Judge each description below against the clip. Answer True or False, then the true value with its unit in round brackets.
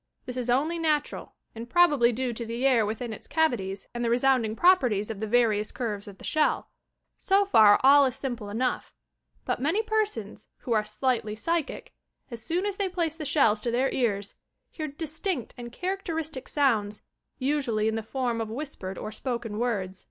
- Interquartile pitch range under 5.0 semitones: False (5.6 semitones)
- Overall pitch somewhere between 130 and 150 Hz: False (245 Hz)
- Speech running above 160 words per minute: True (190 wpm)